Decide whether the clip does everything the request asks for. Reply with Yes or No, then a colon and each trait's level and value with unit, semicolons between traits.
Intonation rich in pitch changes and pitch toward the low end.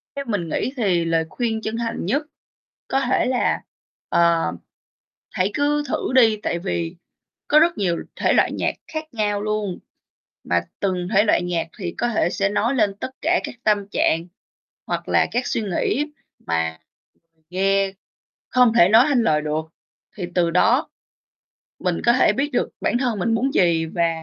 No: wide, 5.9 semitones; high, 205 Hz